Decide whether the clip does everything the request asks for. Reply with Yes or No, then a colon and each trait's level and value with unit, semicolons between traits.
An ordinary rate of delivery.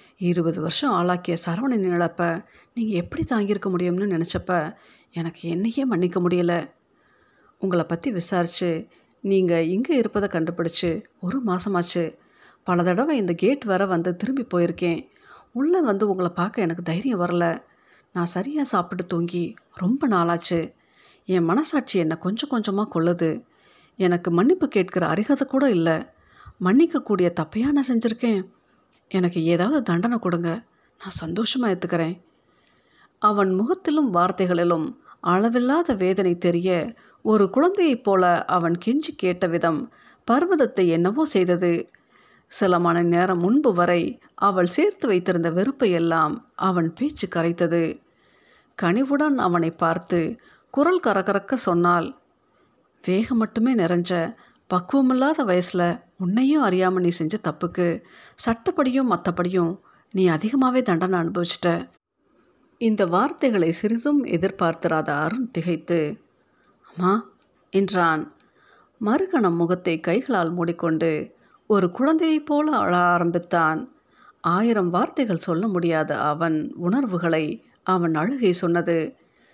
Yes: average, 110 wpm